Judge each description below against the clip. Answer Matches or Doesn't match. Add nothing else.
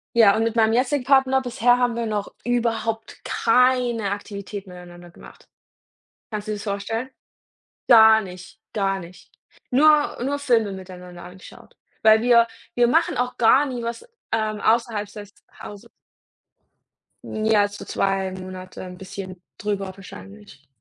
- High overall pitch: Matches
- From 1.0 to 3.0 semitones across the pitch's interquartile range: Doesn't match